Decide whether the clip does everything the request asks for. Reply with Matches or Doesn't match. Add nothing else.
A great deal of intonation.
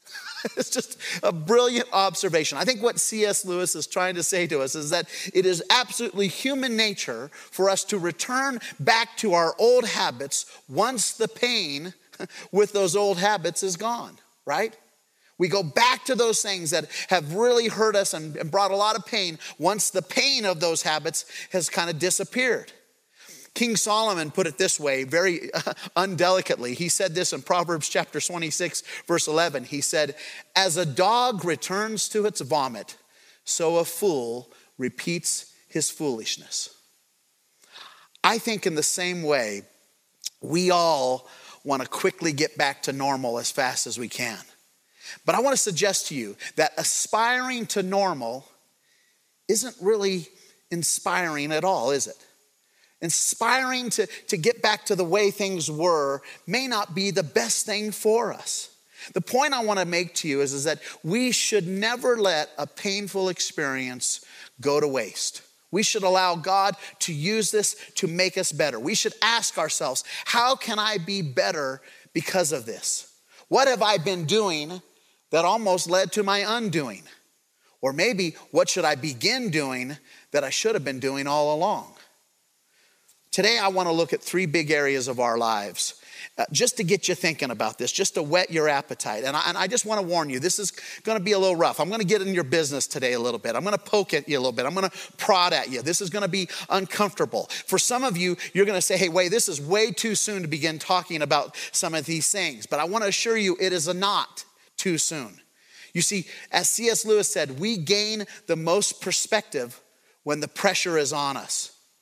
Doesn't match